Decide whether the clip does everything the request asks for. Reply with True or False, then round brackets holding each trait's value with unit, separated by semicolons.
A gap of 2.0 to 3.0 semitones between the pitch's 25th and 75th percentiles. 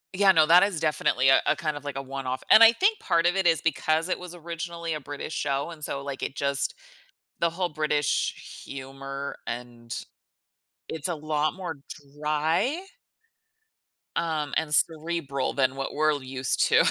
False (3.5 semitones)